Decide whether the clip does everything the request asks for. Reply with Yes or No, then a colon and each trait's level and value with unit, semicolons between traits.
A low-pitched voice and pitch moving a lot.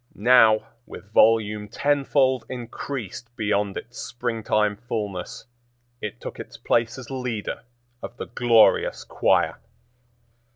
No: low, 115 Hz; average, 2.7 semitones